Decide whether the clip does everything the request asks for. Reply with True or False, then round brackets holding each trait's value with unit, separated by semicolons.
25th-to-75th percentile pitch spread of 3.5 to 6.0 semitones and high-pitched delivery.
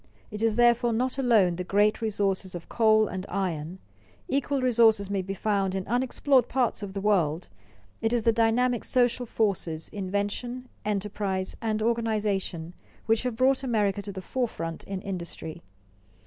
True (3.8 semitones; 210 Hz)